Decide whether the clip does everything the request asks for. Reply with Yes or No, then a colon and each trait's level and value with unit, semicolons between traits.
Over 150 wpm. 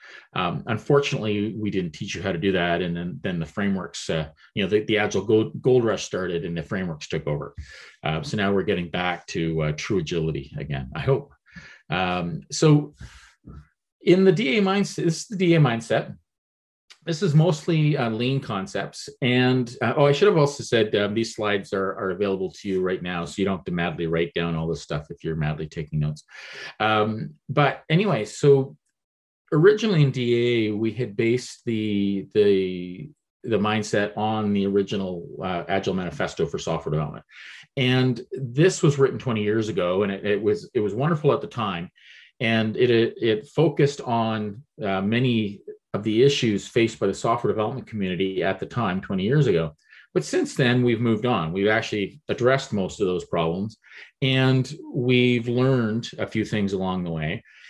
Yes: average, 185 wpm